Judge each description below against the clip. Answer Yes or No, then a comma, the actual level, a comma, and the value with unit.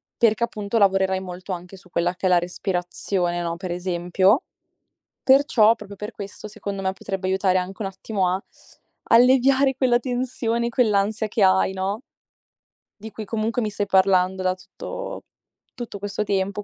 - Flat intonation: No, average, 3.2 semitones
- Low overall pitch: No, high, 200 Hz